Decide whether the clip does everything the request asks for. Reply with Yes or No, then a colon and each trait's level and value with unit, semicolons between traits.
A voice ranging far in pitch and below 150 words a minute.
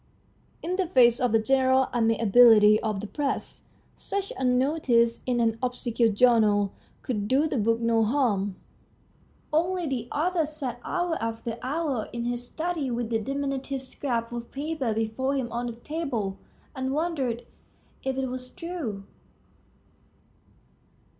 No: average, 3.6 semitones; average, 140 wpm